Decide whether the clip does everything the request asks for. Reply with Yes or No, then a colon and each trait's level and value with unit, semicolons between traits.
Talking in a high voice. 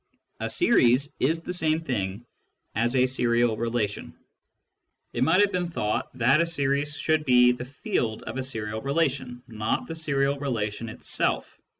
No: low, 130 Hz